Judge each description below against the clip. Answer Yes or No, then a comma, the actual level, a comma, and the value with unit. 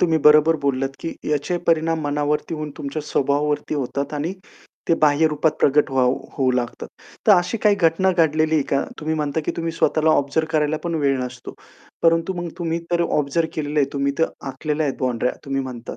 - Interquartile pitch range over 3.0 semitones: No, average, 2.7 semitones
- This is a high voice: No, medium, 150 Hz